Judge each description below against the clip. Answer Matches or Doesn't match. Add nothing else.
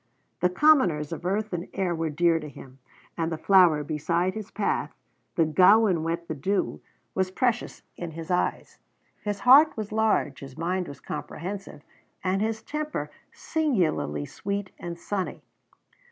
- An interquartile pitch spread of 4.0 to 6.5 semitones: Matches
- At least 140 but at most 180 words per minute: Matches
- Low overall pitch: Doesn't match